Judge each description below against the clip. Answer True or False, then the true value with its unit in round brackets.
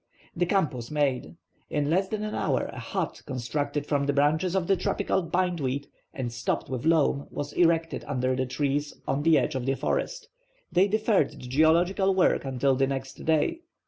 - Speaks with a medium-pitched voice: True (150 Hz)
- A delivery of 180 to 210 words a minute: True (185 wpm)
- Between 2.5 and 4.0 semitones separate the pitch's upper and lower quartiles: False (4.7 semitones)